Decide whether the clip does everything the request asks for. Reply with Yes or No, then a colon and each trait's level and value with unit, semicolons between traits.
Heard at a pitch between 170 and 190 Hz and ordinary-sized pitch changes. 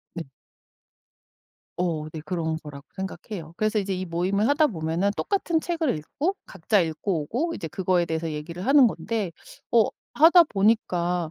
No: medium, 185 Hz; wide, 5.9 semitones